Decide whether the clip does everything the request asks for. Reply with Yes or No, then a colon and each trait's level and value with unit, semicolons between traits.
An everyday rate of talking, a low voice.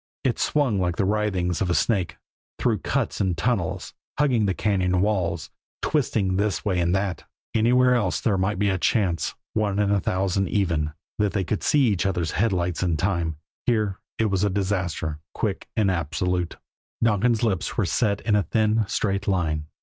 Yes: average, 175 wpm; low, 100 Hz